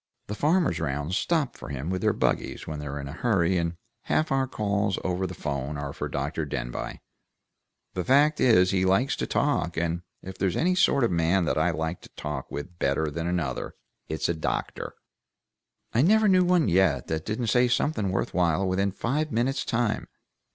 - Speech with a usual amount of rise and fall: No, wide, 7.4 semitones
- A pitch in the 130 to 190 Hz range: No, very low, 95 Hz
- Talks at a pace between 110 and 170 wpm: No, average, 195 wpm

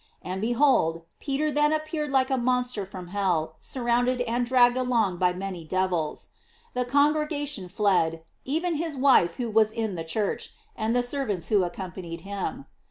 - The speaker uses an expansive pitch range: Yes, wide, 6.2 semitones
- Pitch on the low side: No, high, 235 Hz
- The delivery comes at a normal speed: Yes, average, 165 wpm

